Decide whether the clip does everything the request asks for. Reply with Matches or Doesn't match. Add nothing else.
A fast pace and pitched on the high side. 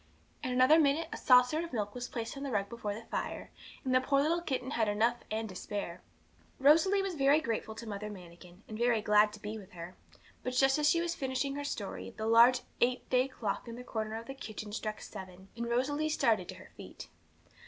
Matches